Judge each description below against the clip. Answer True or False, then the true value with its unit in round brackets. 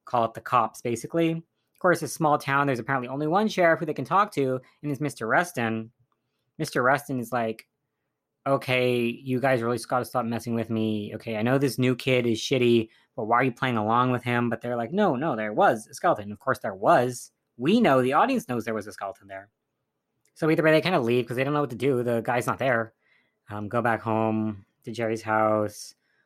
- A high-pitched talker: False (125 Hz)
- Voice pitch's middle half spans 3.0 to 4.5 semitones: True (3.7 semitones)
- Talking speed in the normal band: False (240 wpm)